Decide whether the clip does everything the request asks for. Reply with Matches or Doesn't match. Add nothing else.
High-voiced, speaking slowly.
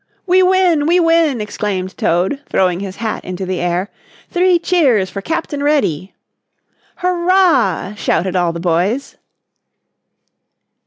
Matches